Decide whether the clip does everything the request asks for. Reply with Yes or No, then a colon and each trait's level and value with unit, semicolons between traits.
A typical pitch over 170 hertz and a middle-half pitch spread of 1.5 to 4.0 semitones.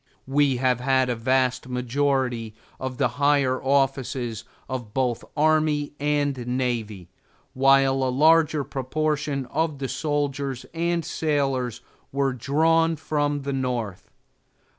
No: low, 135 Hz; narrow, 2.6 semitones